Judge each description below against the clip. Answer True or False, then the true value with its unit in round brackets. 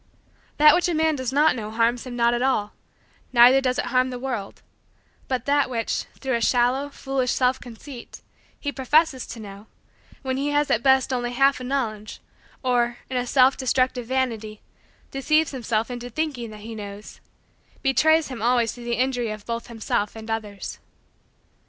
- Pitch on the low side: False (250 Hz)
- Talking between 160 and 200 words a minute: True (175 wpm)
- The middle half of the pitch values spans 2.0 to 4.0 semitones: True (2.6 semitones)